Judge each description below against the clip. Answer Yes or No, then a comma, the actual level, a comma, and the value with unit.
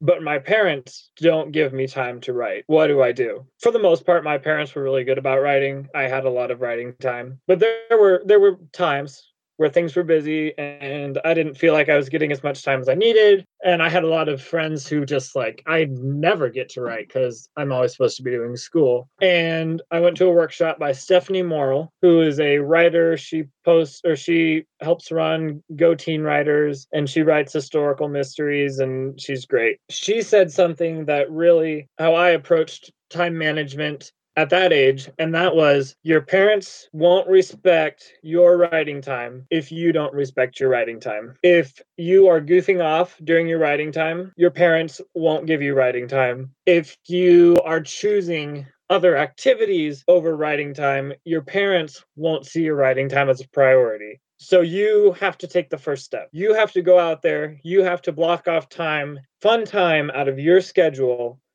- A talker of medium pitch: Yes, medium, 160 Hz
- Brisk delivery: No, average, 195 wpm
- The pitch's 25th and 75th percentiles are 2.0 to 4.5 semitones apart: Yes, average, 4.0 semitones